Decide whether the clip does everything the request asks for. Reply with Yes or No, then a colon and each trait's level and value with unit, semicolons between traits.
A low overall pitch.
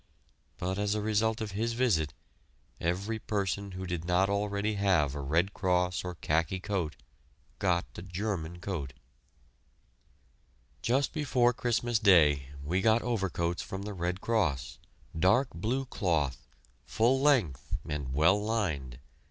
Yes: very low, 95 Hz